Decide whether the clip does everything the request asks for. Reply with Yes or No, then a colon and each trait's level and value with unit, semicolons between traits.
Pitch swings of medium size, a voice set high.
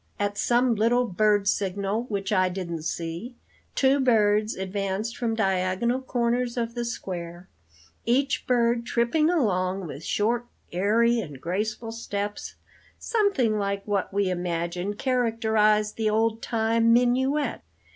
Yes: average, 3.5 semitones; high, 215 Hz